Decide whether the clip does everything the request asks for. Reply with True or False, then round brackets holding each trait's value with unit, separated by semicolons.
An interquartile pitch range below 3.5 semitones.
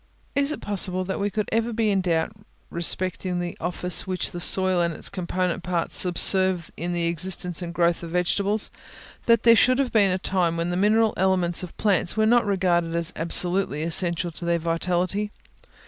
True (2.6 semitones)